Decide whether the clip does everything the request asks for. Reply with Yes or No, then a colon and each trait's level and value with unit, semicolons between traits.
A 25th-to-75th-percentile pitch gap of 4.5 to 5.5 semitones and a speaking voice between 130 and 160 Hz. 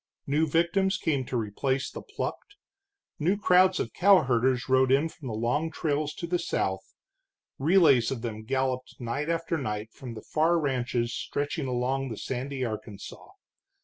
Yes: average, 4.9 semitones; low, 135 Hz